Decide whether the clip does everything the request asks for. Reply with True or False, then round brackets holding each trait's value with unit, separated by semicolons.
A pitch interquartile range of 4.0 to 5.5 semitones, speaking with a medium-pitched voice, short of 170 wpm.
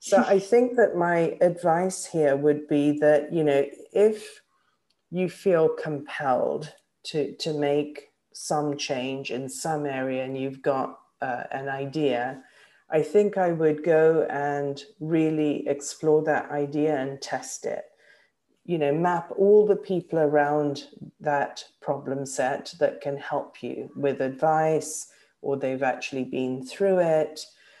False (3.4 semitones; 150 Hz; 140 wpm)